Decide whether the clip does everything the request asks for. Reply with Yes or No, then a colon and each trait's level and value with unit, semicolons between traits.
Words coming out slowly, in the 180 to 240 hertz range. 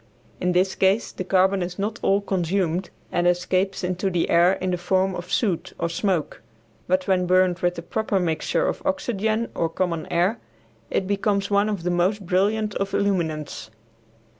No: average, 175 wpm; medium, 185 Hz